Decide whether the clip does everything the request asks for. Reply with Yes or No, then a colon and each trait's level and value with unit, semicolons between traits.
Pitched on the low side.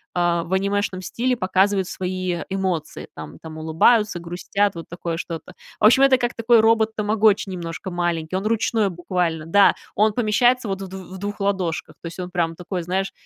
No: high, 190 Hz